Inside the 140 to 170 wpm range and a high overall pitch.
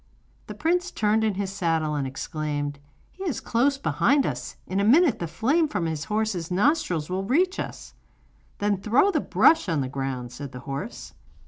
No: average, 185 wpm; high, 195 Hz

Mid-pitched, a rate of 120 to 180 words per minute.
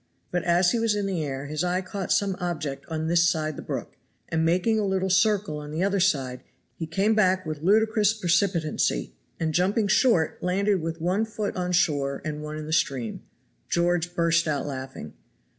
No: medium, 175 Hz; average, 190 wpm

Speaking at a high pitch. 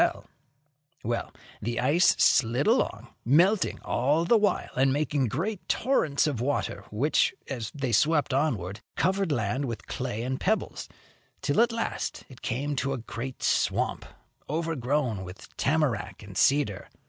No: low, 135 Hz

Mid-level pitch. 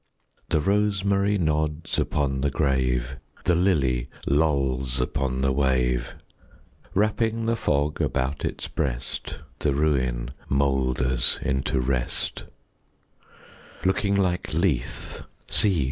No: very low, 70 Hz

